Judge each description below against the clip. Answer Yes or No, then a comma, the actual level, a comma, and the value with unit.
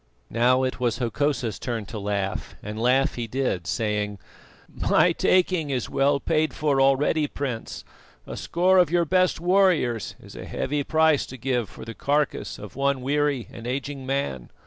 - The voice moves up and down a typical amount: Yes, average, 4.3 semitones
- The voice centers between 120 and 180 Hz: Yes, low, 135 Hz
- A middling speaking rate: Yes, average, 170 wpm